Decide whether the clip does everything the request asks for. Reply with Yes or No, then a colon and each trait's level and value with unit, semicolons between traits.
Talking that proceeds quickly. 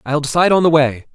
Yes: fast, 260 wpm